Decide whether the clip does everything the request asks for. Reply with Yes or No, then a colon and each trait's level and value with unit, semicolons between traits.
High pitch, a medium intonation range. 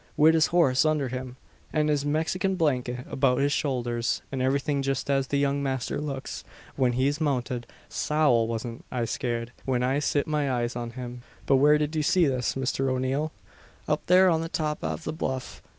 No: low, 135 Hz; average, 3.2 semitones